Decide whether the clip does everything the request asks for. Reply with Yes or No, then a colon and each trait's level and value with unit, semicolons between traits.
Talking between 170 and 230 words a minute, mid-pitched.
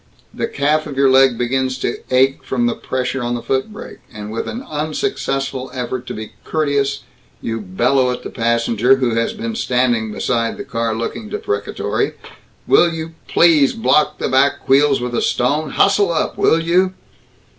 No: average, 175 wpm; low, 130 Hz